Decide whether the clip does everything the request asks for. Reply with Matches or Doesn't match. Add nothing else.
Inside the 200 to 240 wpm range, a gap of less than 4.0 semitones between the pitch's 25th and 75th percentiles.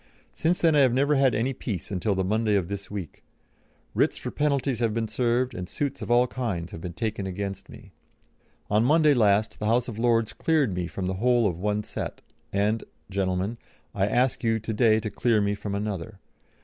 Matches